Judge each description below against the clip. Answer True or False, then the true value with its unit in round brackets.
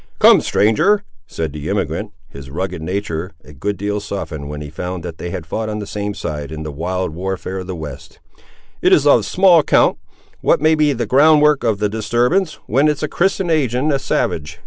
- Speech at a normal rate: False (210 wpm)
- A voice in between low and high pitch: False (100 Hz)